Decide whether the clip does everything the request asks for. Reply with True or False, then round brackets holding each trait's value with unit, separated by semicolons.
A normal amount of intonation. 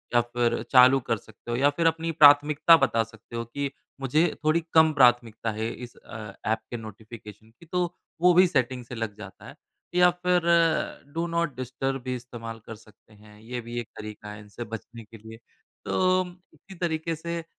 False (6.1 semitones)